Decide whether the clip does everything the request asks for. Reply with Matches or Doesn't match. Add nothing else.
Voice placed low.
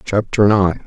Matches